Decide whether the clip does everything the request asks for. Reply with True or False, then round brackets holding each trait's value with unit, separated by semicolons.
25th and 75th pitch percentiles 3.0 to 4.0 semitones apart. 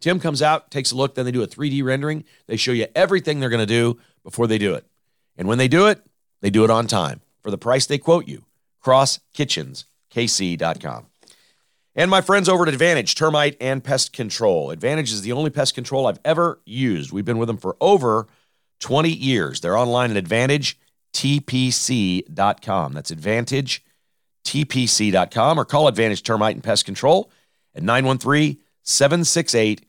False (5.1 semitones)